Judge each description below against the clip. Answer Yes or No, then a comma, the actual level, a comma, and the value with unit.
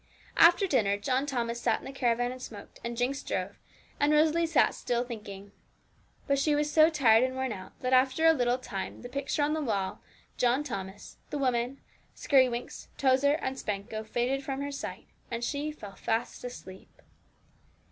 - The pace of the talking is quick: No, average, 175 wpm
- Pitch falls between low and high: No, very high, 255 Hz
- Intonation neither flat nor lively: Yes, average, 3.4 semitones